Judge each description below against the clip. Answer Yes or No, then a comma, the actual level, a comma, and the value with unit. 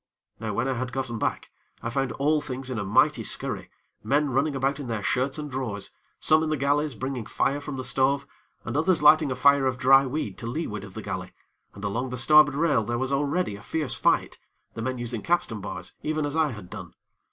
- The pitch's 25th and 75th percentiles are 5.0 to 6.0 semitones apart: No, average, 3.6 semitones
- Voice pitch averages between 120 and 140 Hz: Yes, low, 135 Hz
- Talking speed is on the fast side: Yes, fast, 225 wpm